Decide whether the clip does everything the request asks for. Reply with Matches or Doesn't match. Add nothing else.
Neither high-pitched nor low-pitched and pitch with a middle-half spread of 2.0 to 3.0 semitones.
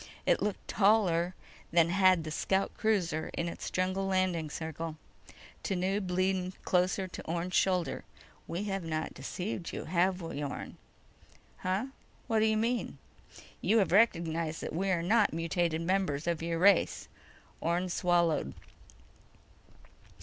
Matches